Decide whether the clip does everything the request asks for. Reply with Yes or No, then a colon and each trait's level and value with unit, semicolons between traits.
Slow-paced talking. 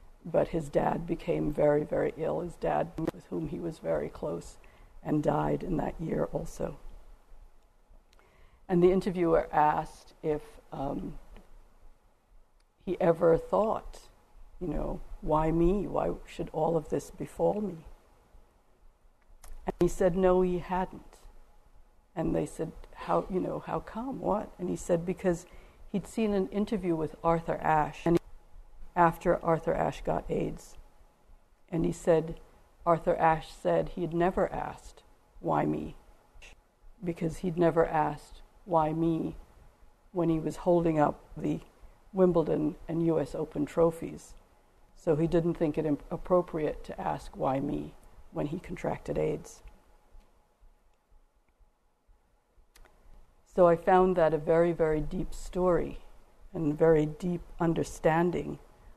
Yes: slow, 130 wpm